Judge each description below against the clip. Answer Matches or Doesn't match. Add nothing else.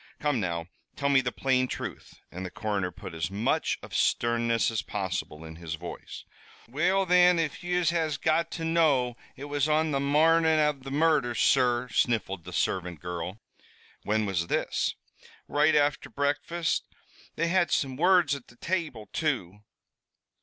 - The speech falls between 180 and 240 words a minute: Doesn't match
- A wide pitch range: Matches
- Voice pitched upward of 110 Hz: Matches